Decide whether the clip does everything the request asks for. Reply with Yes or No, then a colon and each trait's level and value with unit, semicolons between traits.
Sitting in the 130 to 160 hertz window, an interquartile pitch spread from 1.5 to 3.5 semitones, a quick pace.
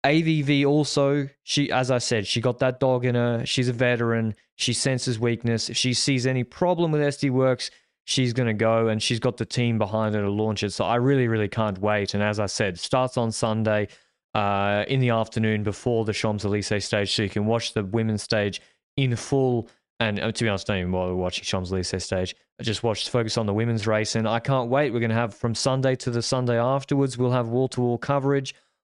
No: low, 115 Hz; average, 3.2 semitones; fast, 225 wpm